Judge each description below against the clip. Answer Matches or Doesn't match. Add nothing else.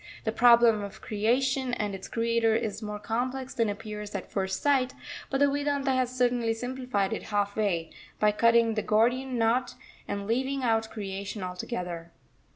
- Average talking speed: Matches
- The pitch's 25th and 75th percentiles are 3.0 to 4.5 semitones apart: Matches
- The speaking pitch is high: Matches